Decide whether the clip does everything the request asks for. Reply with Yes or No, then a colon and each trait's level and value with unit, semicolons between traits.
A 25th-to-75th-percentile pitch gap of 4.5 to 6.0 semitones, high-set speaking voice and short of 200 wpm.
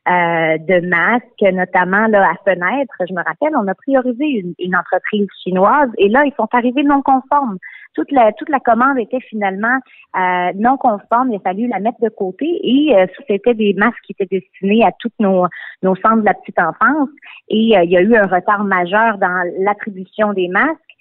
No: average, 5.0 semitones; high, 210 Hz; average, 205 wpm